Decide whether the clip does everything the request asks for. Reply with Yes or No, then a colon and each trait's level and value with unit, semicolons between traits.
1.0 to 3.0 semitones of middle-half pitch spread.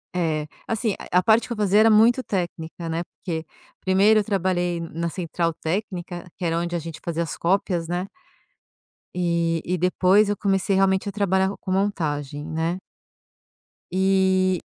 Yes: average, 2.7 semitones